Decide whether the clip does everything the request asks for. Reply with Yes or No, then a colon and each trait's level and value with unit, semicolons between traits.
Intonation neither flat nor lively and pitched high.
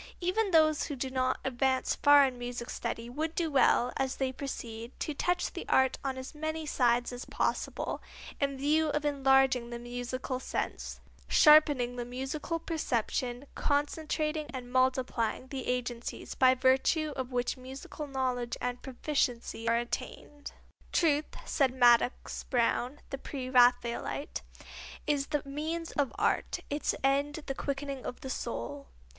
Yes: average, 3.0 semitones; very high, 265 Hz